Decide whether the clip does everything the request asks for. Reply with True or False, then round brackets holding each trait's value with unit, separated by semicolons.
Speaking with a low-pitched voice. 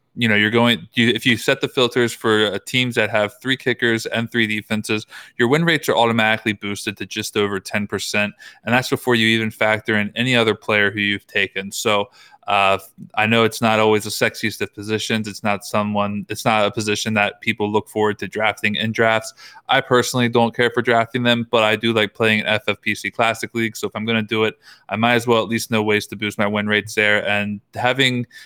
True (110 Hz)